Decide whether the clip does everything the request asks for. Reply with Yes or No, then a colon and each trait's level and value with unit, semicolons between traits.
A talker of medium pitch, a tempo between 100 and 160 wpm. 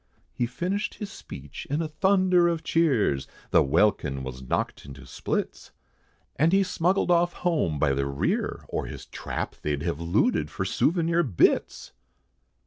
Yes: medium, 145 Hz; average, 150 wpm